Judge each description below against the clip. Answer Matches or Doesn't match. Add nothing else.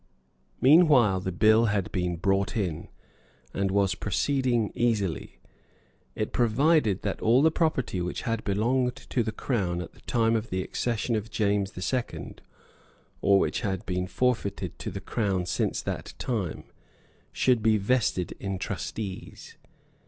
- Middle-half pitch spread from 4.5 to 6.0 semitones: Doesn't match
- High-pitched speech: Doesn't match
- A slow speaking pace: Doesn't match